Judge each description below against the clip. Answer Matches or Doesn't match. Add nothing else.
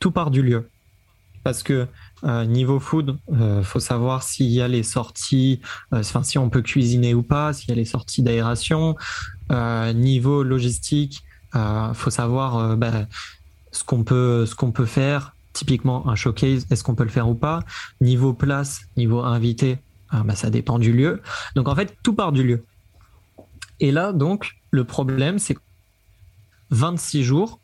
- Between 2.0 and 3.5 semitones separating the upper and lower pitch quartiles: Matches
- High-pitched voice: Doesn't match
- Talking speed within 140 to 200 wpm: Matches